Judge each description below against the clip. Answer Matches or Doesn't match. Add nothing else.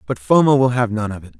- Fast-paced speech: Matches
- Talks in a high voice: Doesn't match